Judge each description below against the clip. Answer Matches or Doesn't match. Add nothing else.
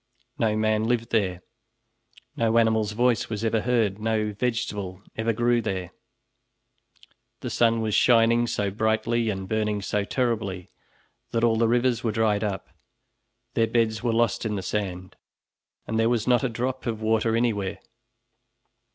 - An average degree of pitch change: Doesn't match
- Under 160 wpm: Matches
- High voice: Doesn't match